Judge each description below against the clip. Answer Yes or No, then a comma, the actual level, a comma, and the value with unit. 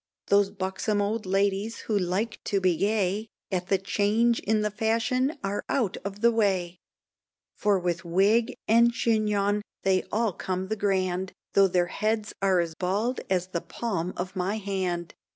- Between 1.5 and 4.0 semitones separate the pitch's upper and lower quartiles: Yes, narrow, 2.6 semitones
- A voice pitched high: Yes, high, 200 Hz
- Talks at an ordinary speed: Yes, average, 165 wpm